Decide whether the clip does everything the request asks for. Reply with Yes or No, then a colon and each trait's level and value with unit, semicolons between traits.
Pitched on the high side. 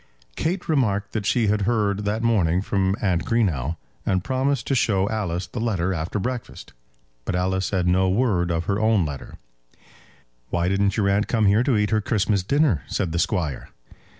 No: low, 100 Hz